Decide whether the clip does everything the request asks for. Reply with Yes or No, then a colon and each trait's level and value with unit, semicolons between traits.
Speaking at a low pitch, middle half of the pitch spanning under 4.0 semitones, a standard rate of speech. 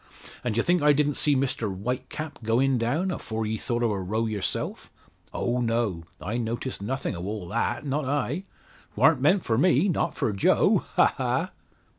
No: low, 120 Hz; average, 4.7 semitones; average, 180 wpm